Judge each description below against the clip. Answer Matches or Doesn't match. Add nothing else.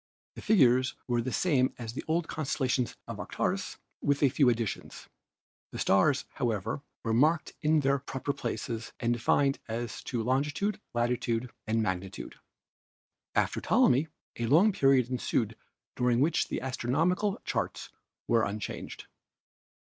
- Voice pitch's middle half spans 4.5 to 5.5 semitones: Doesn't match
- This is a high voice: Doesn't match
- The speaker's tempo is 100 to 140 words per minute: Matches